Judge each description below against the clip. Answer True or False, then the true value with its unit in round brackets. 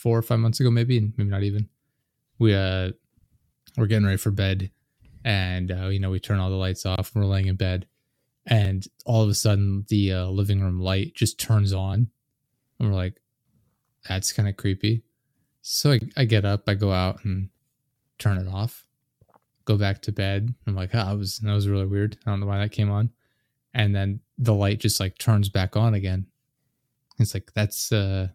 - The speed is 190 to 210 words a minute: True (205 wpm)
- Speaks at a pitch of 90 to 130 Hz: True (105 Hz)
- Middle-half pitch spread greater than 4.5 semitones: False (2.9 semitones)